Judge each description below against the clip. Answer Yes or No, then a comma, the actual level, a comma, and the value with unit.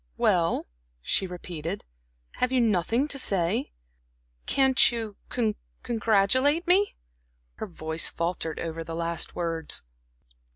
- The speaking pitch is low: No, high, 195 Hz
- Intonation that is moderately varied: No, wide, 7.1 semitones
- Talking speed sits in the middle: No, slow, 110 wpm